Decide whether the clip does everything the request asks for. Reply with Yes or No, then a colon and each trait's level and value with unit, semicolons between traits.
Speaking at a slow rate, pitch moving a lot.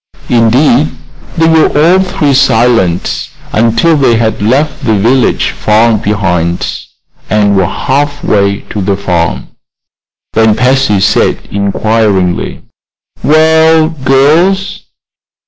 Yes: slow, 105 wpm; wide, 6.3 semitones